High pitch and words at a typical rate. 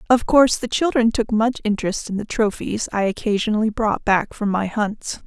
Yes: high, 220 Hz; average, 195 wpm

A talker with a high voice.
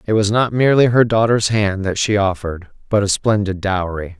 No: low, 105 Hz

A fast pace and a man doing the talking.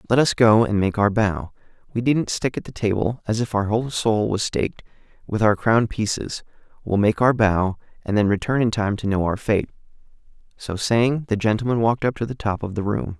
Yes: fast, 220 wpm; male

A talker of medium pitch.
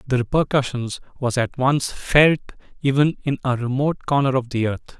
No: low, 130 Hz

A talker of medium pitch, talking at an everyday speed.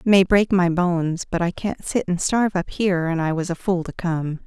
No: medium, 180 Hz; fast, 255 wpm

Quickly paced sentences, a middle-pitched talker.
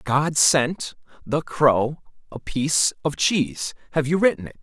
No: average, 155 wpm; medium, 145 Hz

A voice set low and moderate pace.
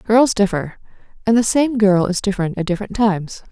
No: high, 205 Hz; average, 190 wpm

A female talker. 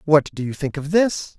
No: male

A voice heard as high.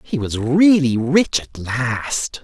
No: low, 135 Hz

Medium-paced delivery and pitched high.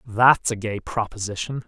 No: average, 145 wpm; low, 110 Hz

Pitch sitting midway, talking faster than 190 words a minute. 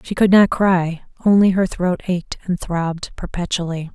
No: medium, 180 Hz; average, 165 wpm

